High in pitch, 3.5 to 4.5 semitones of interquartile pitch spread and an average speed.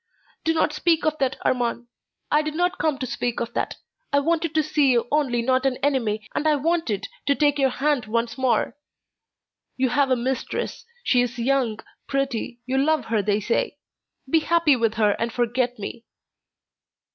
Yes: very high, 260 Hz; average, 4.0 semitones; average, 180 wpm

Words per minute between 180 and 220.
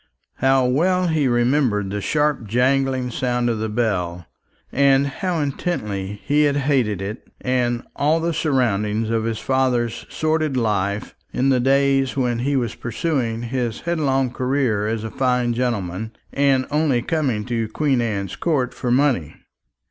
No: average, 150 wpm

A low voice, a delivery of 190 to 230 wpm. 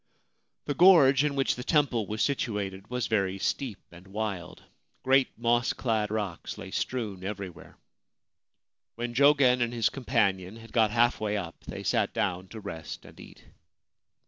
No: low, 115 Hz; average, 160 wpm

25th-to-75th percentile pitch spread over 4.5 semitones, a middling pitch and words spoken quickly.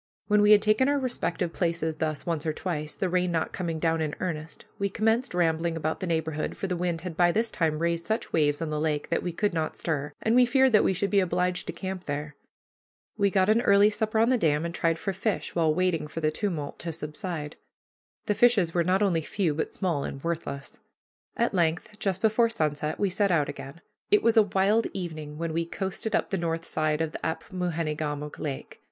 No: average, 4.1 semitones; medium, 170 Hz; fast, 220 wpm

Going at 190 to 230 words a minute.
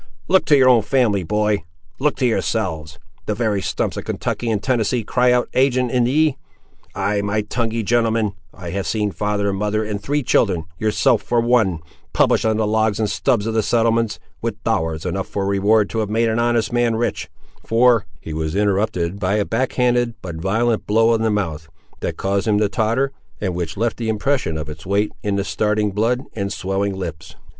Yes: average, 200 wpm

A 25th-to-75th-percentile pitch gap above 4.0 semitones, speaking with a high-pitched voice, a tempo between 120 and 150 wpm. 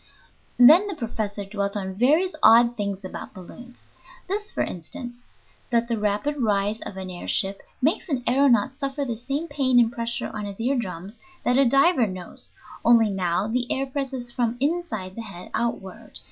No: average, 4.8 semitones; high, 235 Hz; average, 175 wpm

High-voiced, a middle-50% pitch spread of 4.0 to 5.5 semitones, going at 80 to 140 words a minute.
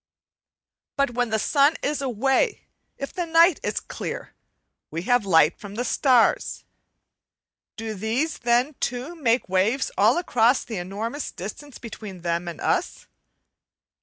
Yes: high, 240 Hz; average, 5.2 semitones; slow, 135 wpm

